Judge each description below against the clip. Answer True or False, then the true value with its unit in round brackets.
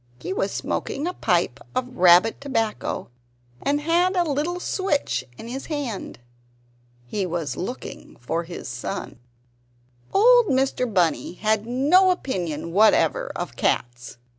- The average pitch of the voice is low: False (245 Hz)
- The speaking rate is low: True (130 wpm)